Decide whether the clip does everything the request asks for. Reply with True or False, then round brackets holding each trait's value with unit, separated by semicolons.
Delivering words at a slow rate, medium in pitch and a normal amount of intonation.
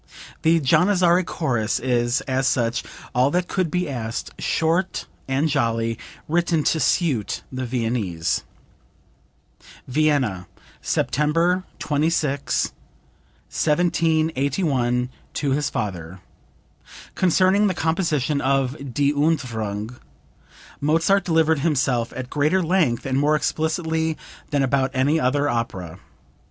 True (105 wpm; 145 Hz; 4.6 semitones)